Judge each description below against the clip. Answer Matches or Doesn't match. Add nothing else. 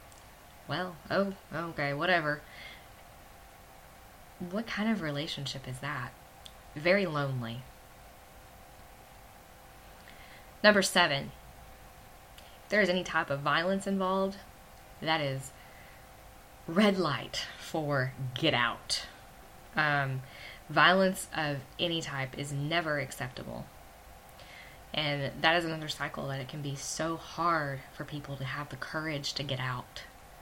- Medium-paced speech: Doesn't match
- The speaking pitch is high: Doesn't match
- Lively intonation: Matches